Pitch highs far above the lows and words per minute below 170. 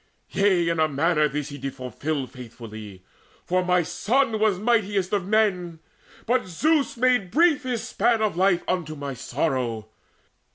Yes: wide, 7.3 semitones; average, 155 wpm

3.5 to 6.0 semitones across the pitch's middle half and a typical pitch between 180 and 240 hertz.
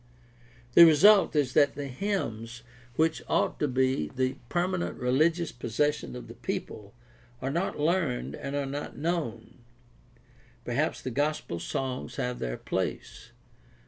No: average, 4.6 semitones; medium, 140 Hz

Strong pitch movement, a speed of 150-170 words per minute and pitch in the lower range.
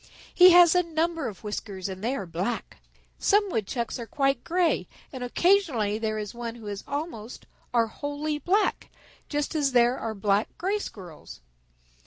No: wide, 7.3 semitones; average, 165 wpm; high, 245 Hz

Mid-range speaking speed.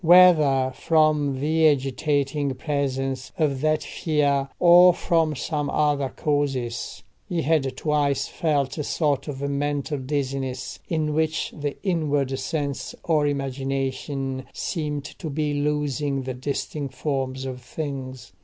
No: slow, 125 wpm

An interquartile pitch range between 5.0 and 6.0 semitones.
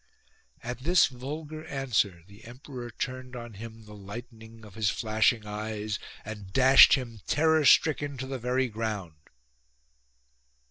No: average, 3.6 semitones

